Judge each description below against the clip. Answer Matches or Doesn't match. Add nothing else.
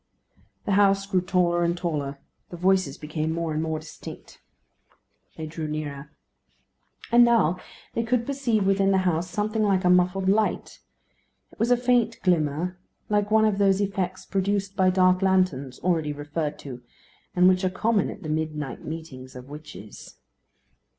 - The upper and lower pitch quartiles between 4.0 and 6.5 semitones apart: Matches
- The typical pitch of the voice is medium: Matches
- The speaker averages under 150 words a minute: Doesn't match